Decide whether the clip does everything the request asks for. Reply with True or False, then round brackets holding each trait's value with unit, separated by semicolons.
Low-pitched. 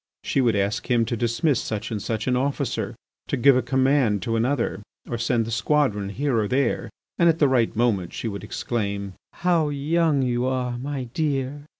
True (125 Hz)